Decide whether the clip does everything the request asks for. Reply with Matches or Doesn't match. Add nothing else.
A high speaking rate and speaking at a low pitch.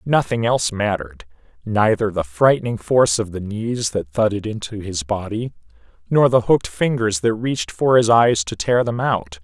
Doesn't match